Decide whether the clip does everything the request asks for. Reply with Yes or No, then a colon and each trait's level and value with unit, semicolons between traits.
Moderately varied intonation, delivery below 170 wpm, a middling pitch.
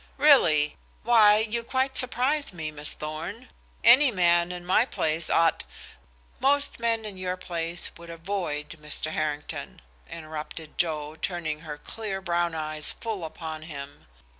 No: wide, 6.0 semitones; average, 140 wpm; medium, 170 Hz